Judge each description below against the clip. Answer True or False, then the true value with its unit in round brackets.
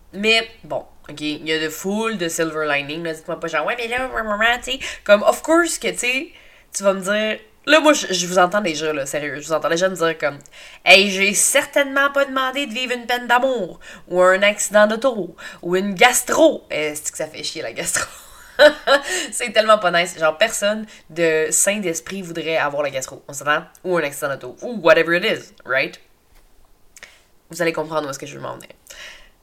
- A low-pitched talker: False (190 Hz)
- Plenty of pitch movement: True (7.2 semitones)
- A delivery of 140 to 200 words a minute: False (210 wpm)